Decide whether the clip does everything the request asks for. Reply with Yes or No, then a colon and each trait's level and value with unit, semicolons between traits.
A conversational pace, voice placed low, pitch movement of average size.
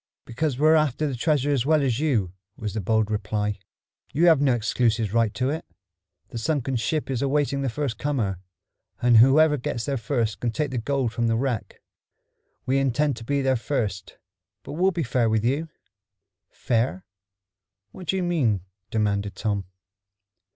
Yes: average, 170 wpm; low, 125 Hz; average, 4.5 semitones